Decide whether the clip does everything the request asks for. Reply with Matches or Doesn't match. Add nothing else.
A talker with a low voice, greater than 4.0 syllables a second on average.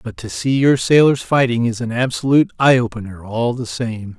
Matches